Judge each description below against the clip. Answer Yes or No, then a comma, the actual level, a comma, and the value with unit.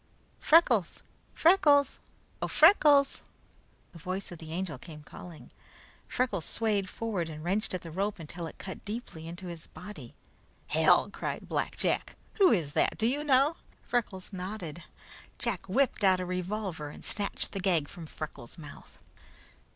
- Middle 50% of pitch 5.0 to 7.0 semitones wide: Yes, average, 5.3 semitones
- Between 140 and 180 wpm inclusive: Yes, average, 150 wpm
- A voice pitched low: No, high, 190 Hz